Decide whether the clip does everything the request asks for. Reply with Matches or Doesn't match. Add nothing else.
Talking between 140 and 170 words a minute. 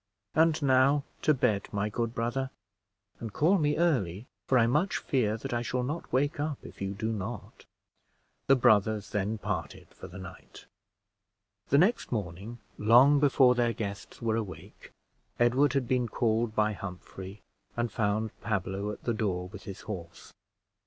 Matches